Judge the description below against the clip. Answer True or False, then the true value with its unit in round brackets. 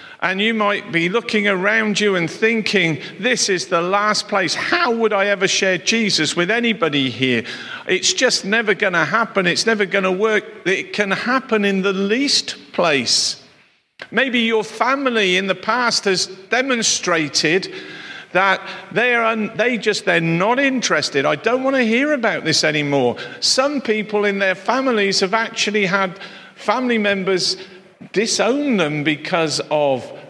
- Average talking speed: True (165 wpm)